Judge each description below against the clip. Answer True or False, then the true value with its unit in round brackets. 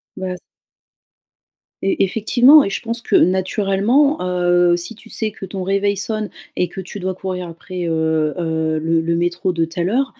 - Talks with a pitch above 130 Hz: True (185 Hz)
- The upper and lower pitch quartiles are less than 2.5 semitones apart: False (2.9 semitones)